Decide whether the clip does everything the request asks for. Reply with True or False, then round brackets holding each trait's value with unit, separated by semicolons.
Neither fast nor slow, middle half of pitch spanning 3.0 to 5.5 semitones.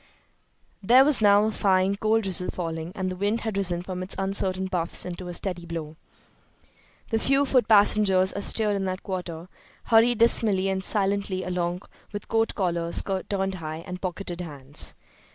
False (165 wpm; 2.6 semitones)